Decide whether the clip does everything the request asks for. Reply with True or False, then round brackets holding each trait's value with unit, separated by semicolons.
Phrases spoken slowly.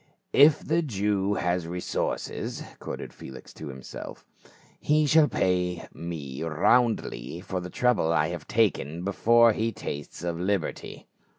True (130 wpm)